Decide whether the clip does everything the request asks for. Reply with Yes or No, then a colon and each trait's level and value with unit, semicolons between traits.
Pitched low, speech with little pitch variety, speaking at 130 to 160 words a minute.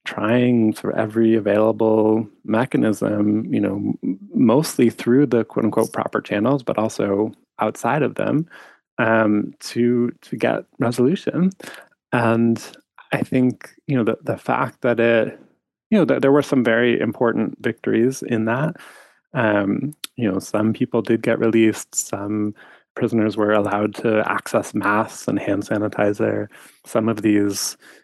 Yes: low, 115 Hz; narrow, 2.2 semitones; average, 140 wpm